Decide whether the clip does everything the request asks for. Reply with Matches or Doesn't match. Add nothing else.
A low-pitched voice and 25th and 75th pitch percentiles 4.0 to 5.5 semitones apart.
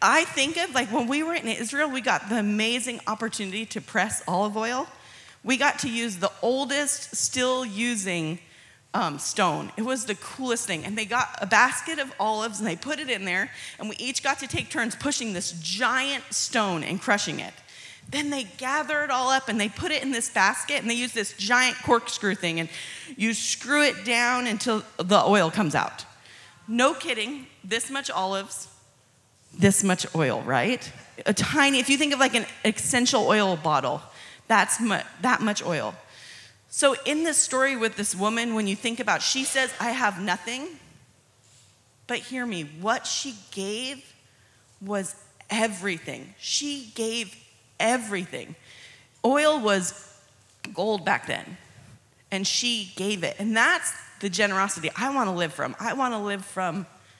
Doesn't match